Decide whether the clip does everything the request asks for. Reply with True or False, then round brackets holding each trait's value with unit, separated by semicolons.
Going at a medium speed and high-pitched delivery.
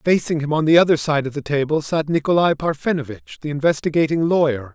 False (190 wpm; 150 Hz)